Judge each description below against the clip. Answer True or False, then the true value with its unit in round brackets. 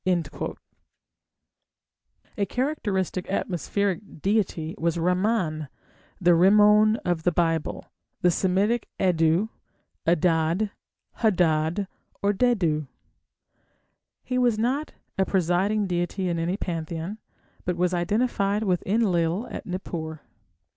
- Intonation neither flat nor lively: True (3.8 semitones)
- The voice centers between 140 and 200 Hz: True (185 Hz)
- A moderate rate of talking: False (100 wpm)